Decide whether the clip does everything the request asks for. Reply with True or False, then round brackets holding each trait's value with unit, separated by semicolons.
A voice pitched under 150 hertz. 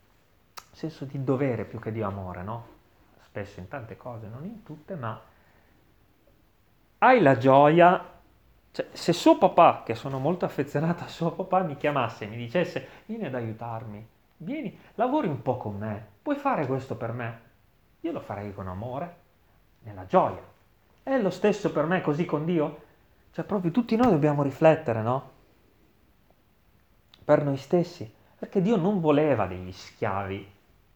True (135 Hz)